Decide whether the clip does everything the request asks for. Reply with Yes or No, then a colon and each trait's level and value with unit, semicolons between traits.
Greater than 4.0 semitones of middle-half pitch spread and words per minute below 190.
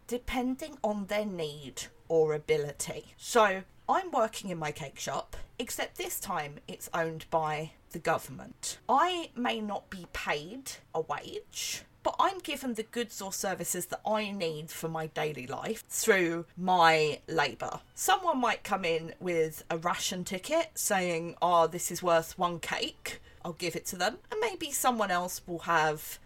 Yes: average, 5.2 semitones; average, 160 wpm